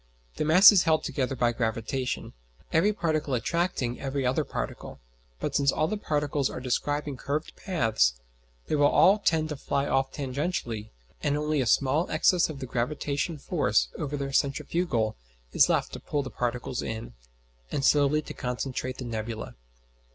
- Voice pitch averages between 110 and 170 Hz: Yes, medium, 140 Hz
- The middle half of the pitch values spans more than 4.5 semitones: No, average, 3.5 semitones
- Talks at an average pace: Yes, average, 160 wpm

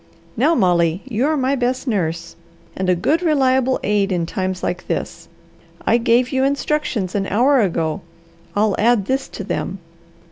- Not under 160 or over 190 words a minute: Yes, average, 165 wpm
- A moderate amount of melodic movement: No, wide, 6.0 semitones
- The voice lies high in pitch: Yes, high, 230 Hz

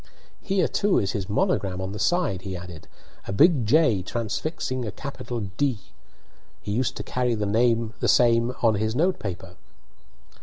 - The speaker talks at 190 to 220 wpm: No, average, 160 wpm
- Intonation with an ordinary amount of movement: Yes, average, 4.6 semitones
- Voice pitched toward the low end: Yes, low, 115 Hz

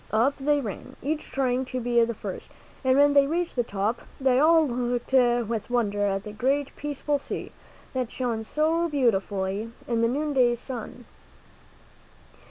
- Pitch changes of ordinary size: Yes, average, 3.6 semitones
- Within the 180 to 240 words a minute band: No, average, 160 wpm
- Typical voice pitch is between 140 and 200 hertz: No, very high, 250 Hz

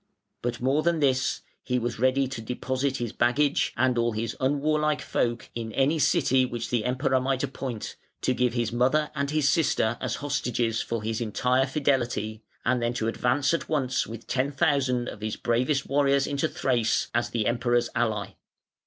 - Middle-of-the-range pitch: No, low, 125 Hz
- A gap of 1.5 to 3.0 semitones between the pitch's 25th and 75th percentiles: Yes, average, 2.7 semitones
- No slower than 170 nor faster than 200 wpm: Yes, average, 180 wpm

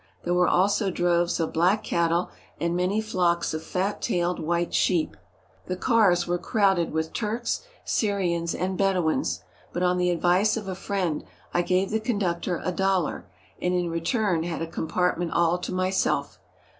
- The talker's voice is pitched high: No, medium, 180 Hz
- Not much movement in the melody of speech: Yes, narrow, 2.1 semitones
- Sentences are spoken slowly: No, average, 170 wpm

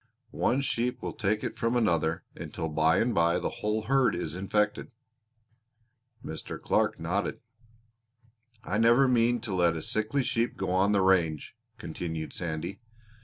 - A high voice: No, low, 100 Hz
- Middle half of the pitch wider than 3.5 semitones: Yes, wide, 5.5 semitones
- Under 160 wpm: Yes, average, 150 wpm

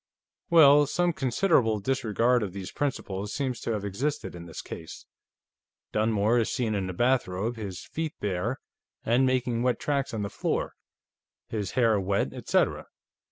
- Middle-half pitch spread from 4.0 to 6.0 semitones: Yes, average, 4.6 semitones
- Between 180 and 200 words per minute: No, average, 155 wpm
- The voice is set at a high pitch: No, low, 115 Hz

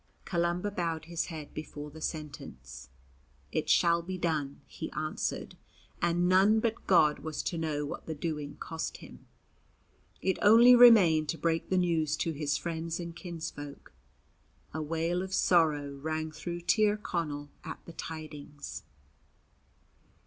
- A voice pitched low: No, medium, 165 Hz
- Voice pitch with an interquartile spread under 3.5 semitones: Yes, narrow, 2.6 semitones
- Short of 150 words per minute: Yes, average, 140 wpm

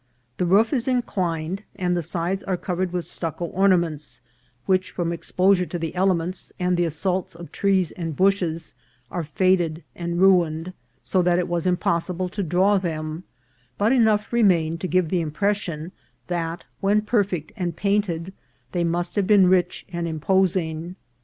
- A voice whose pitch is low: No, medium, 180 Hz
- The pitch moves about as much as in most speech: No, narrow, 2.3 semitones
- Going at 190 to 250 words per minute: No, average, 165 wpm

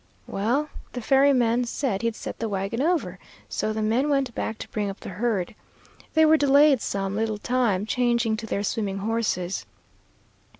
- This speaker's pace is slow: No, average, 170 wpm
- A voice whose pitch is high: Yes, high, 230 Hz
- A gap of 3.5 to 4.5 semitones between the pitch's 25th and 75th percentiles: Yes, average, 3.9 semitones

